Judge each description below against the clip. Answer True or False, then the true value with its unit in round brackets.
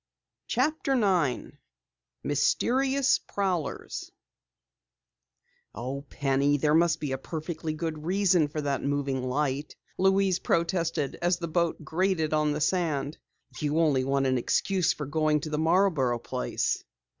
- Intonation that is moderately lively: True (3.7 semitones)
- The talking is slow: True (130 wpm)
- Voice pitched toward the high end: False (155 Hz)